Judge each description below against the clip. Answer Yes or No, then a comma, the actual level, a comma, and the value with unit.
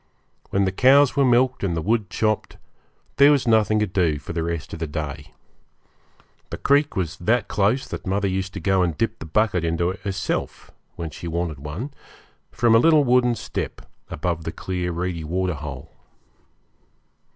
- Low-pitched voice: Yes, very low, 95 Hz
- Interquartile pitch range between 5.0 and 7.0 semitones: Yes, wide, 5.4 semitones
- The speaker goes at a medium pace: Yes, average, 175 wpm